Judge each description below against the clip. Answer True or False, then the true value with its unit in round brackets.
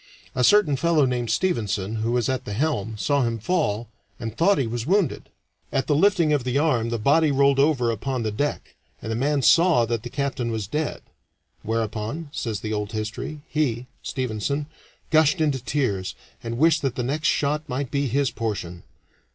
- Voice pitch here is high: False (130 Hz)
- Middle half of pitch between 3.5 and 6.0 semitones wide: True (4.7 semitones)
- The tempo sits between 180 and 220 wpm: True (185 wpm)